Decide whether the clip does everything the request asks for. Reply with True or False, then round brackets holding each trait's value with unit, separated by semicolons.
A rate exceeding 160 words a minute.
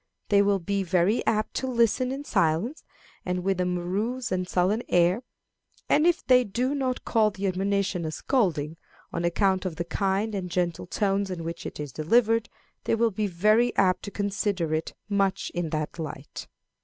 True (180 wpm)